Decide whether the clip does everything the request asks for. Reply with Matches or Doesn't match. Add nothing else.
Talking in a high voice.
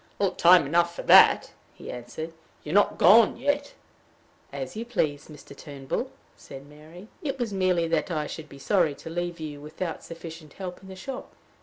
Doesn't match